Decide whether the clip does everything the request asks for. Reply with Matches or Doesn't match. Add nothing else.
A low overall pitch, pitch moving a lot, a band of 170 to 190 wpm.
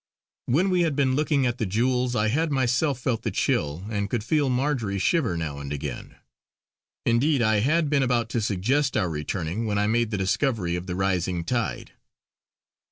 Matches